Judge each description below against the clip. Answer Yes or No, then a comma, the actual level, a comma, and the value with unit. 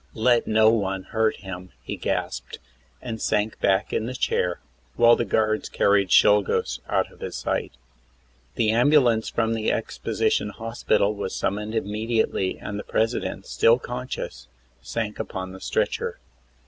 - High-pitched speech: No, low, 110 Hz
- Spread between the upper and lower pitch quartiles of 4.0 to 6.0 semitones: No, narrow, 2.4 semitones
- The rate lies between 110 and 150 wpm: Yes, average, 145 wpm